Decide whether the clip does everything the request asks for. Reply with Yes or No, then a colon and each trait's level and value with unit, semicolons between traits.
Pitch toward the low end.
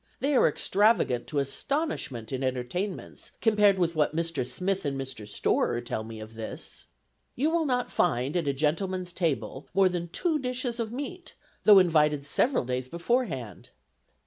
No: medium, 170 Hz